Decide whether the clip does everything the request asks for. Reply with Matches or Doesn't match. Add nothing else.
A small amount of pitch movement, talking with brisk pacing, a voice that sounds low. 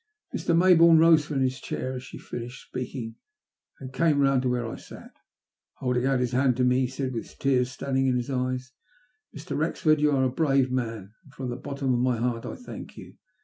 Matches